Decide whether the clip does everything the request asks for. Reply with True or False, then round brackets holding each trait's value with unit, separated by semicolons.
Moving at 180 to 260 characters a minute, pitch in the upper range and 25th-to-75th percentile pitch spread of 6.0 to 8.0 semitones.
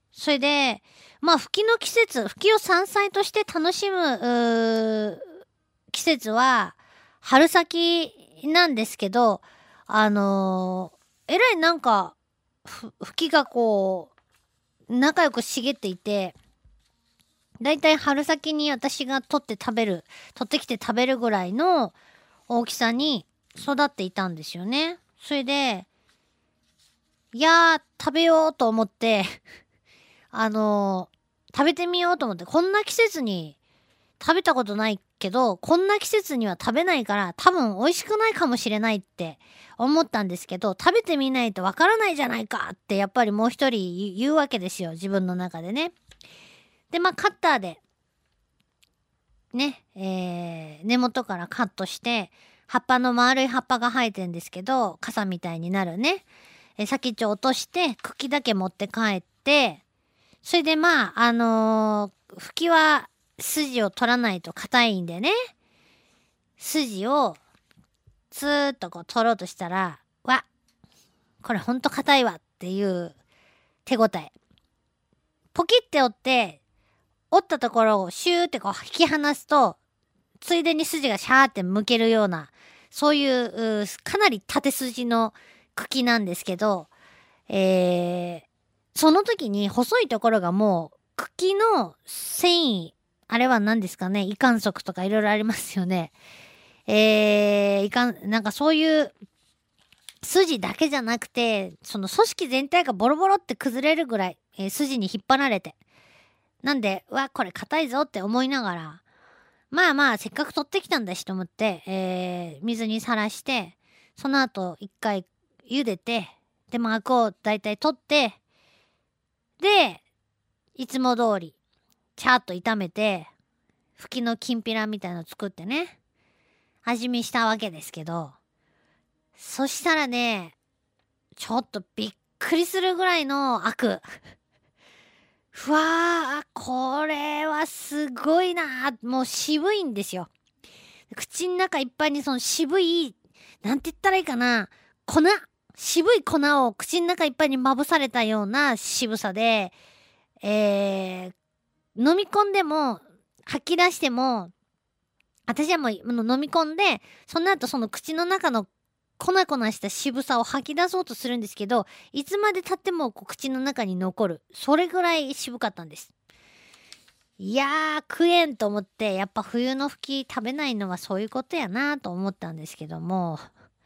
False (270 characters per minute; 240 Hz; 7.1 semitones)